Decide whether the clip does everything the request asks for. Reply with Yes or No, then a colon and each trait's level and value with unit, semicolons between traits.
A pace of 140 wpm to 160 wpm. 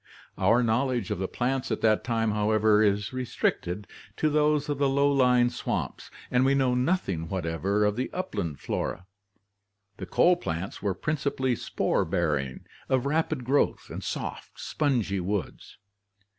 Yes: average, 150 wpm